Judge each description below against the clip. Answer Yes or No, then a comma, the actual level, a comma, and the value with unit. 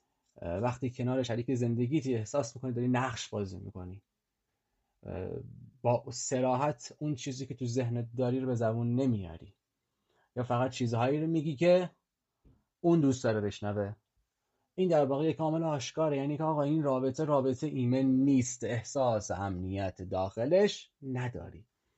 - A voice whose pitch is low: Yes, low, 125 Hz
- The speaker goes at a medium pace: Yes, average, 140 wpm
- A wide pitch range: No, average, 4.0 semitones